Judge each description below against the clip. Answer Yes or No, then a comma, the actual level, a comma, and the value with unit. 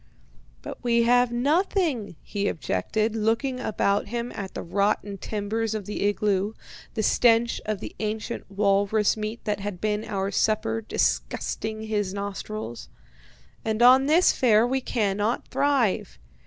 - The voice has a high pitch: Yes, high, 215 Hz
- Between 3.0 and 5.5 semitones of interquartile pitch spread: No, narrow, 2.6 semitones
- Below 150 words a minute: Yes, average, 140 wpm